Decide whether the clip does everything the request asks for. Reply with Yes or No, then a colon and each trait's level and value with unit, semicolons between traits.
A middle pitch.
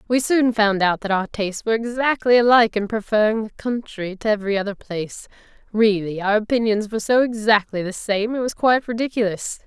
No: high, 215 Hz